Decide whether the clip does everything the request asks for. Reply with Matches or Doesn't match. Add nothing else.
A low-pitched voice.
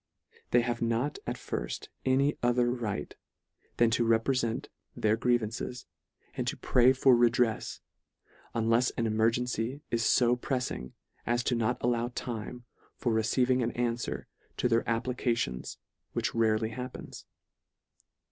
Matches